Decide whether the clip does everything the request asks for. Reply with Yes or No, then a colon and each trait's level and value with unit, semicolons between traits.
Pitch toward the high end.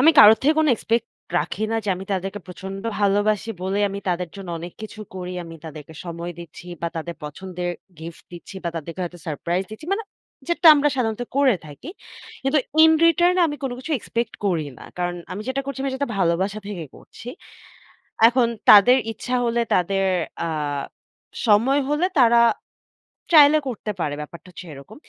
Yes: high, 205 Hz